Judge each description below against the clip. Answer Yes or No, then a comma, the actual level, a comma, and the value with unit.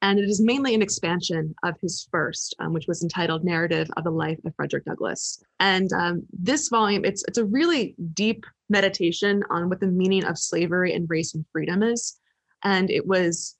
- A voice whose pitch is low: No, medium, 185 Hz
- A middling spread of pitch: Yes, average, 3.3 semitones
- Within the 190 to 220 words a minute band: Yes, average, 195 wpm